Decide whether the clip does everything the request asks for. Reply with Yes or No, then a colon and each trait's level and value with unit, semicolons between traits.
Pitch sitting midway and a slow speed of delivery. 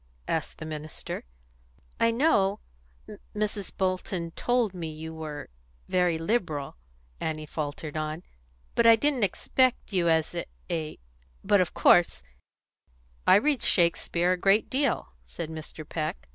Yes: medium, 175 Hz; slow, 130 wpm